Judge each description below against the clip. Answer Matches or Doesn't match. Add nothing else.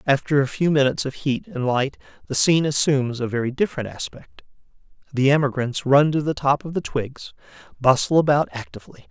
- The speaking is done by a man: Matches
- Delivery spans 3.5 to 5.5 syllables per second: Doesn't match